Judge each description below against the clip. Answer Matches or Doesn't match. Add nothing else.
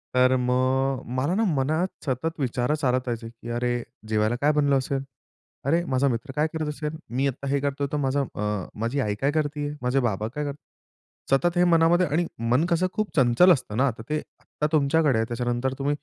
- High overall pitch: Doesn't match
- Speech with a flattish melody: Doesn't match